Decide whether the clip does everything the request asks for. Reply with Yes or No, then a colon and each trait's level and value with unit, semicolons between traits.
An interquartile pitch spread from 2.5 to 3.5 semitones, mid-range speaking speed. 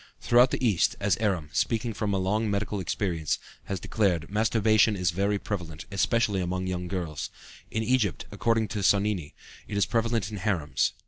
Yes: average, 3.2 semitones; average, 170 wpm